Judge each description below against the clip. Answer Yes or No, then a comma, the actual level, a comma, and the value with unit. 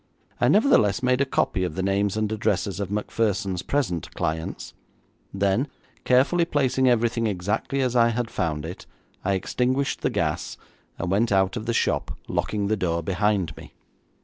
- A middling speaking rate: Yes, average, 165 wpm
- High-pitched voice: No, low, 105 Hz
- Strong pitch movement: No, average, 4.5 semitones